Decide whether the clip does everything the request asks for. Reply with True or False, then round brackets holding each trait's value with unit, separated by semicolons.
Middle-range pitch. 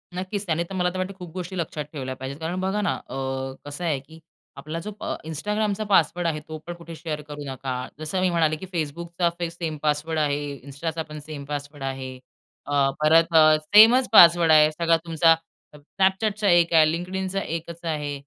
True (165 Hz)